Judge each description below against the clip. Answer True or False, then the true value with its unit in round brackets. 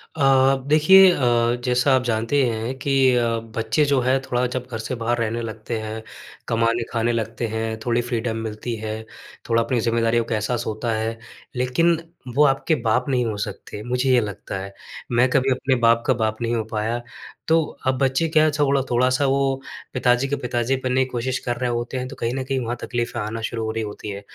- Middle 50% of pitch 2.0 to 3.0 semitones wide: True (2.4 semitones)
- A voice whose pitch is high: False (120 Hz)